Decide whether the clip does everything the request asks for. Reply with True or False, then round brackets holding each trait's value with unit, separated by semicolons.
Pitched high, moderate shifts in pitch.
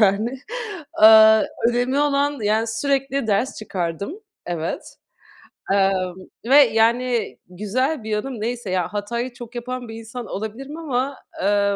True (230 Hz; 3.8 semitones)